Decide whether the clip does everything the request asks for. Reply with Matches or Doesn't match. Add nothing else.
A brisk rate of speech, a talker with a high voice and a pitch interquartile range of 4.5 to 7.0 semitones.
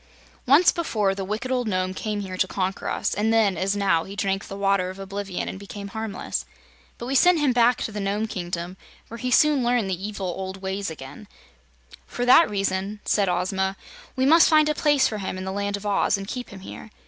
Doesn't match